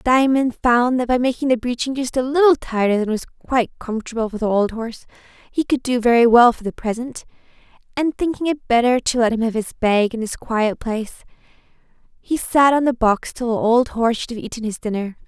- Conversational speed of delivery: No, fast, 215 wpm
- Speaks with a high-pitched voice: Yes, high, 240 Hz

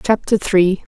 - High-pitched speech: Yes, high, 195 Hz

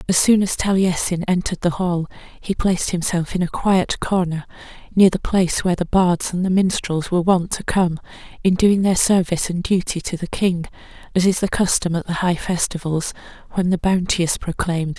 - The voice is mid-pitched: Yes, medium, 180 Hz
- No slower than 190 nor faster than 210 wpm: Yes, average, 195 wpm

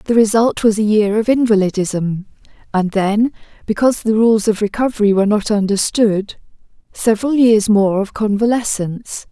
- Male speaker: No, female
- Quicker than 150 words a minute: No, average, 140 wpm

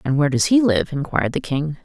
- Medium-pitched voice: Yes, medium, 160 Hz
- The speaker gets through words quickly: Yes, fast, 260 wpm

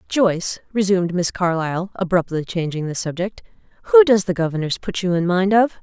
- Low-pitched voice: No, medium, 185 Hz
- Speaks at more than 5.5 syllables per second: Yes, 5.7 syllables/s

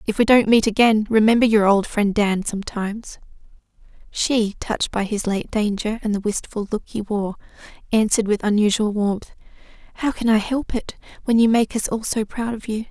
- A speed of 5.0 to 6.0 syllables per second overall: Yes, 5.3 syllables/s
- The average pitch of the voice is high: Yes, high, 215 Hz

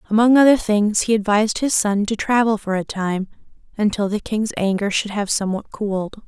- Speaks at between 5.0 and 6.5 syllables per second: Yes, 5.4 syllables/s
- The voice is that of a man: No, female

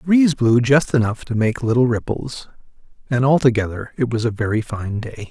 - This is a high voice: No, low, 120 Hz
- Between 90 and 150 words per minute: No, average, 190 wpm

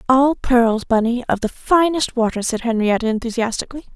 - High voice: Yes, high, 240 Hz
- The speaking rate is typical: Yes, average, 150 wpm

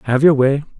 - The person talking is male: Yes, male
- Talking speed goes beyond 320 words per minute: No, fast, 225 wpm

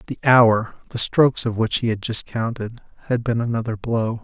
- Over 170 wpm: Yes, average, 200 wpm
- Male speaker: Yes, male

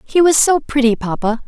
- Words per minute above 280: No, fast, 205 wpm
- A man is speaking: No, female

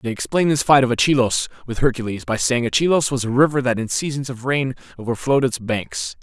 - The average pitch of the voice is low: Yes, low, 125 Hz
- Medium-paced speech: No, fast, 210 wpm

